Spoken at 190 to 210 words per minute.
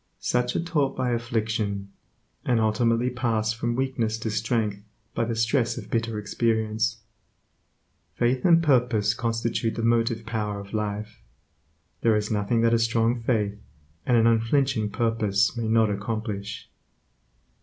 No: average, 140 wpm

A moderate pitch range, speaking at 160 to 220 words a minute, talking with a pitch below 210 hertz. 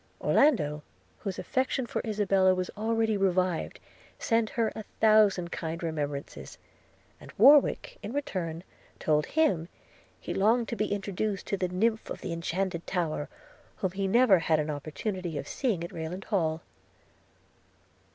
No: average, 4.7 semitones; average, 140 wpm; high, 190 Hz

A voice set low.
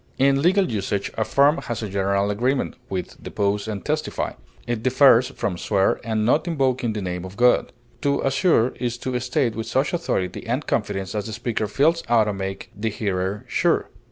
Yes: low, 115 Hz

